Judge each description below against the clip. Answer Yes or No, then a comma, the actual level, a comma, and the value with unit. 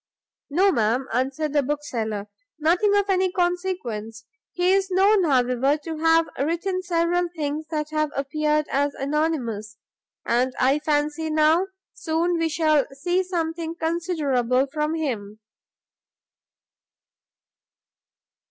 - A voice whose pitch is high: Yes, very high, 310 Hz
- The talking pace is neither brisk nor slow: No, slow, 115 wpm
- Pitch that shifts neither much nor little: Yes, average, 4.1 semitones